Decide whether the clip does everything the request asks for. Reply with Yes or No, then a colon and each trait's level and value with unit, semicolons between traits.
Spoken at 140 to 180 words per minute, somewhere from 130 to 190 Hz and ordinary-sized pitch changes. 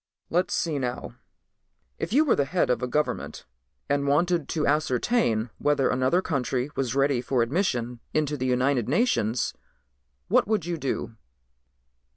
Yes: average, 150 wpm; medium, 140 Hz; average, 4.9 semitones